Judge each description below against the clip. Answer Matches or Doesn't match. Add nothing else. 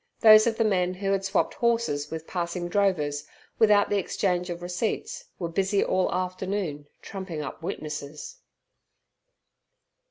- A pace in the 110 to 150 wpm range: Matches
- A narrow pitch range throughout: Doesn't match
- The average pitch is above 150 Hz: Matches